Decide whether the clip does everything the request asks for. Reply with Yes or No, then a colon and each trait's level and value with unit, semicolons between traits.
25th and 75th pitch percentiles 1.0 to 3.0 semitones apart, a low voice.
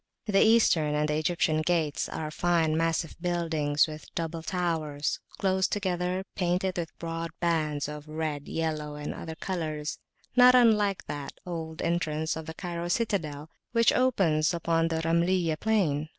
No: narrow, 2.5 semitones; medium, 165 Hz